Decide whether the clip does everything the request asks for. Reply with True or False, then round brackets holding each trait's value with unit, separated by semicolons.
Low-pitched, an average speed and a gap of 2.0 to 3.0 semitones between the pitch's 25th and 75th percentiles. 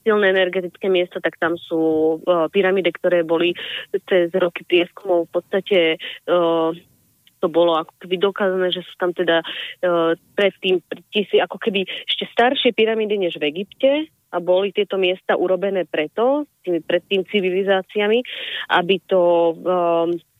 False (180 Hz; 145 wpm; 2.7 semitones)